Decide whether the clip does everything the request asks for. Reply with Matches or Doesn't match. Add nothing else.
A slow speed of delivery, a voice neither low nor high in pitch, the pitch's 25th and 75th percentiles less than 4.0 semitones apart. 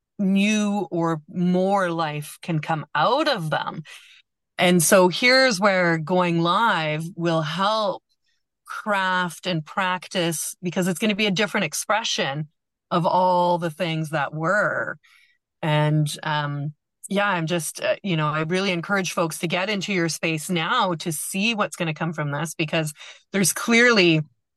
Doesn't match